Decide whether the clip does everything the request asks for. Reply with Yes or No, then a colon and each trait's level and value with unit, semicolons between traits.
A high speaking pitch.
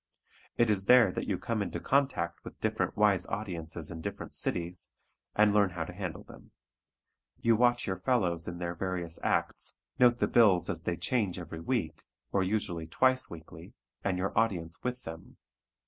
No: very low, 95 Hz